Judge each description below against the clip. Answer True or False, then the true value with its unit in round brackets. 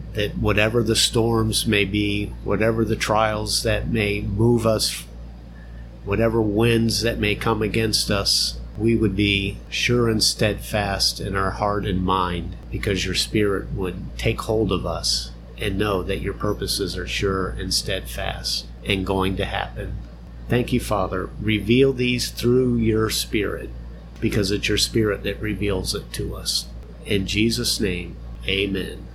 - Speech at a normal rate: True (150 wpm)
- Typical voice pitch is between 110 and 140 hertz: False (100 Hz)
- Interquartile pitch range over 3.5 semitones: False (3.1 semitones)